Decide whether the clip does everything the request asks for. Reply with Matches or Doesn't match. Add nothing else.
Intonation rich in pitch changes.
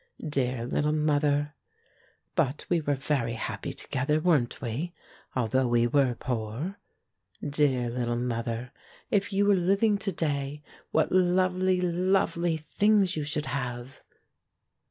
Matches